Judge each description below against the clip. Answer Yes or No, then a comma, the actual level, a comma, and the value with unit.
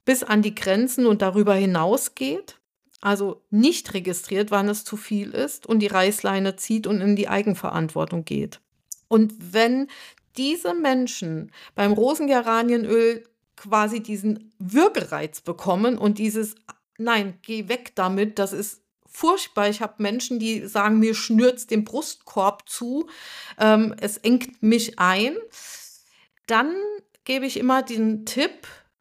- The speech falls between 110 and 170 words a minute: Yes, average, 135 wpm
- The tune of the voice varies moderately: Yes, average, 3.8 semitones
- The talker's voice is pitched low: No, high, 220 Hz